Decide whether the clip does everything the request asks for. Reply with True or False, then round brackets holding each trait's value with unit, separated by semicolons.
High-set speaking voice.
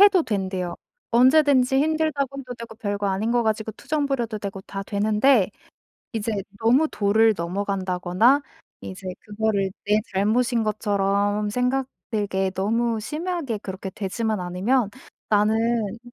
True (220 Hz)